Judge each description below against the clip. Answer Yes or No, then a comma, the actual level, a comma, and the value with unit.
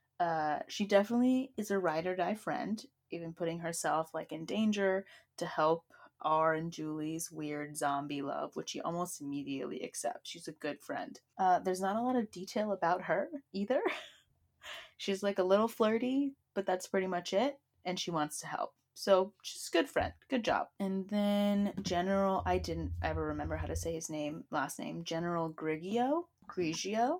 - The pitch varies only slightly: No, average, 4.5 semitones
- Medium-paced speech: Yes, average, 180 wpm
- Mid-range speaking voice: Yes, medium, 180 Hz